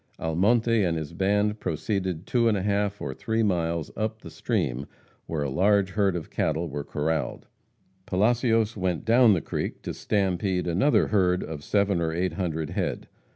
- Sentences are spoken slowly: No, average, 170 wpm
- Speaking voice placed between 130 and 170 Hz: No, very low, 95 Hz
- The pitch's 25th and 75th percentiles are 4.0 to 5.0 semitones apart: Yes, average, 4.3 semitones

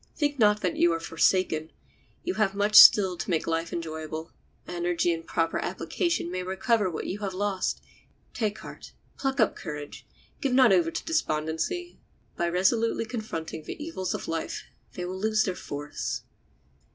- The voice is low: No, medium, 185 Hz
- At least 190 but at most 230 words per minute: No, average, 165 wpm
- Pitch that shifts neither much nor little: Yes, average, 4.8 semitones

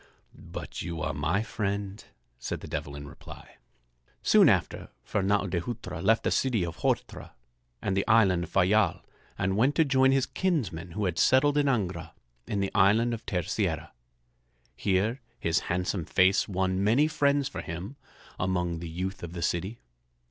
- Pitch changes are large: No, average, 4.7 semitones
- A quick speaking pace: No, average, 165 wpm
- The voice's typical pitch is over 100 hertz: No, very low, 95 Hz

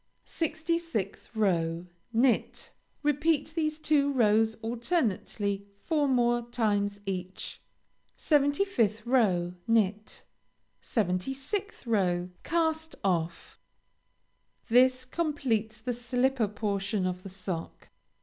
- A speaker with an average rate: No, slow, 90 wpm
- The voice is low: No, high, 230 Hz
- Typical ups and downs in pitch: No, wide, 6.1 semitones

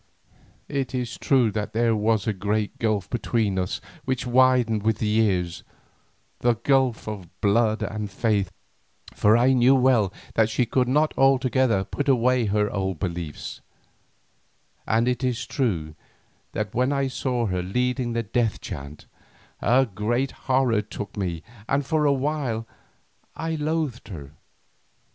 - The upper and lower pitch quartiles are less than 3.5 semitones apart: No, average, 3.8 semitones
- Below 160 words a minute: Yes, average, 145 wpm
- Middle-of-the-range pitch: No, low, 115 Hz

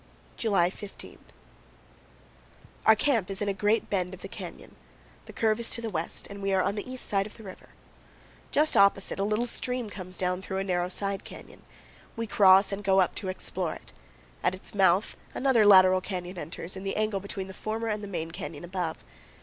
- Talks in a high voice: Yes, high, 195 Hz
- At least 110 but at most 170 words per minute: No, fast, 205 wpm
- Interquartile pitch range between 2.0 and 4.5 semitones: Yes, narrow, 2.4 semitones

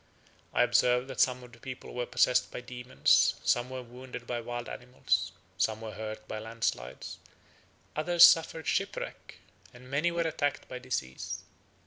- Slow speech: No, average, 155 wpm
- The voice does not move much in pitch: Yes, narrow, 2.1 semitones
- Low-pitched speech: Yes, low, 125 Hz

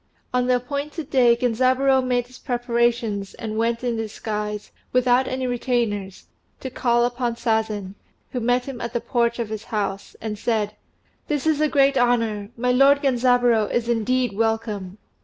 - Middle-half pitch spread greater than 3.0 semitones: No, narrow, 2.4 semitones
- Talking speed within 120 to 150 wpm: No, average, 160 wpm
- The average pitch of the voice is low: No, high, 240 Hz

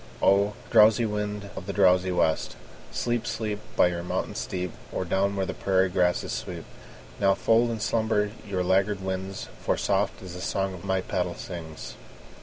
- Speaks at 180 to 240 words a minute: No, average, 170 wpm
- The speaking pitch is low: Yes, very low, 95 Hz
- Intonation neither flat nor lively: No, narrow, 2.2 semitones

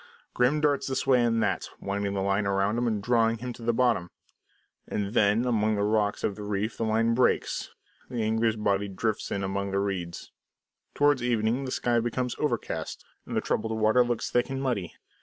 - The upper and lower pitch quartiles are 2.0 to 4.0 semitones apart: Yes, average, 3.2 semitones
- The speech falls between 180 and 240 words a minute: Yes, average, 195 wpm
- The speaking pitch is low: Yes, low, 110 Hz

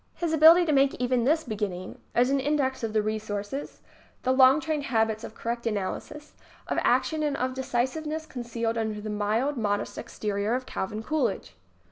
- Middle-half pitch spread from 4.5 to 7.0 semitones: Yes, average, 4.8 semitones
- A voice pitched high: Yes, high, 245 Hz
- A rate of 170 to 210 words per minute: Yes, average, 175 wpm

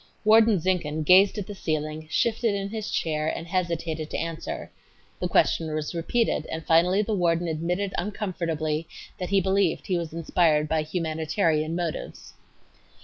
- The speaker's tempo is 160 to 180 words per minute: No, average, 150 wpm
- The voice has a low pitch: No, medium, 170 Hz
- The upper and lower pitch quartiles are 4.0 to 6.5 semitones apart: No, average, 3.5 semitones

